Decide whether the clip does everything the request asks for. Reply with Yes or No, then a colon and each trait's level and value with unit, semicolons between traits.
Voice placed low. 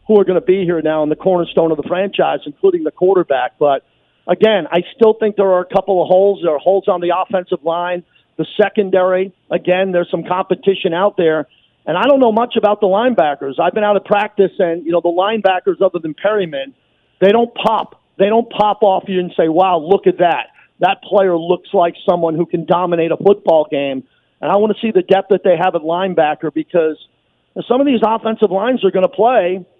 No: medium, 185 Hz